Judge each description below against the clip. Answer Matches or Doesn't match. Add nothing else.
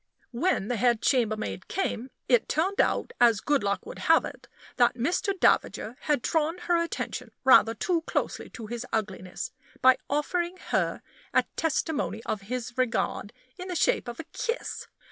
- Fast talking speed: Doesn't match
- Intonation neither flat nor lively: Doesn't match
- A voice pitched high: Matches